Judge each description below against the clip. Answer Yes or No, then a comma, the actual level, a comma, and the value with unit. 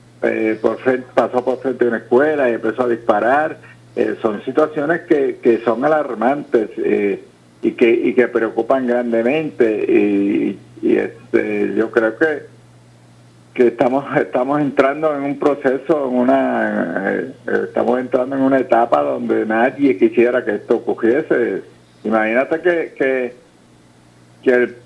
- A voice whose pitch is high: No, low, 125 Hz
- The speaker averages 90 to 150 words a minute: Yes, average, 140 wpm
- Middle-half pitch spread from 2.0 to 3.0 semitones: No, average, 5.0 semitones